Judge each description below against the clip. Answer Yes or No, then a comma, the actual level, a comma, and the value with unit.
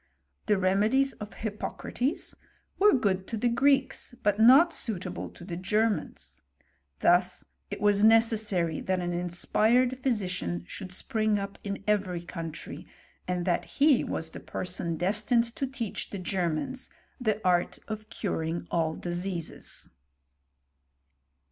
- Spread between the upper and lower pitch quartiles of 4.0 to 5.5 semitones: Yes, average, 4.5 semitones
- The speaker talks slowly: Yes, slow, 130 wpm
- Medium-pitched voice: No, high, 200 Hz